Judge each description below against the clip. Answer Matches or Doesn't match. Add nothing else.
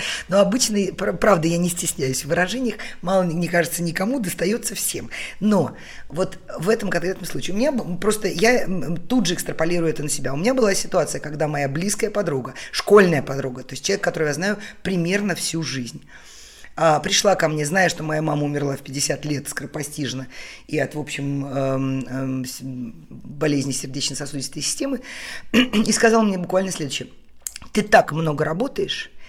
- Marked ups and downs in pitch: Matches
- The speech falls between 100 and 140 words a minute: Doesn't match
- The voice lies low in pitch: Doesn't match